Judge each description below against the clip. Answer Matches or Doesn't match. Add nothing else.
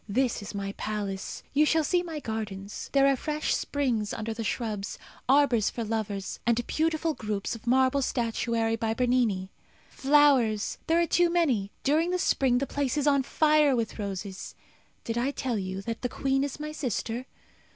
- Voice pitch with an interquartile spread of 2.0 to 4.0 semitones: Doesn't match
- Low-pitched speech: Doesn't match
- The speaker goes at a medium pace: Matches